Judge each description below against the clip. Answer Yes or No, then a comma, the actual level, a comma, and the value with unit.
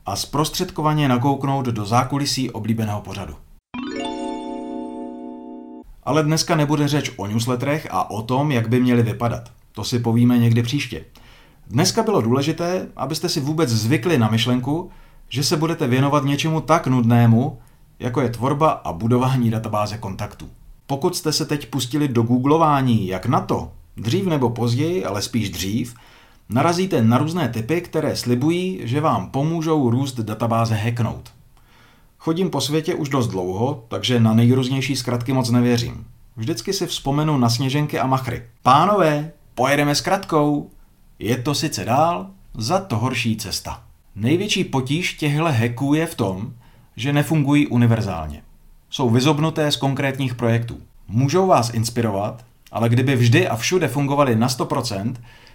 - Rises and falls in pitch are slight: No, average, 4.5 semitones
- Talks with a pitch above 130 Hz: No, low, 125 Hz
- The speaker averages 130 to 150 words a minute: Yes, average, 145 wpm